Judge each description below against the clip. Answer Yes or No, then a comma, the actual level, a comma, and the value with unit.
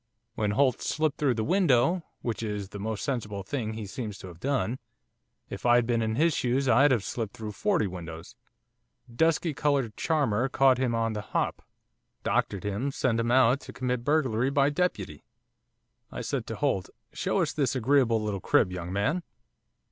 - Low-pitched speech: Yes, low, 120 Hz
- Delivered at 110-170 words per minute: No, average, 180 wpm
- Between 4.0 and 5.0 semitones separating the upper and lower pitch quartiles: Yes, average, 4.7 semitones